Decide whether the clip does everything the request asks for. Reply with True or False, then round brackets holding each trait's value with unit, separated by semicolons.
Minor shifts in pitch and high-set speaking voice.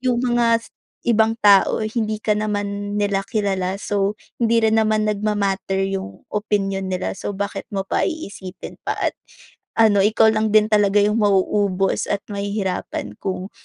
True (1.8 semitones; 205 Hz)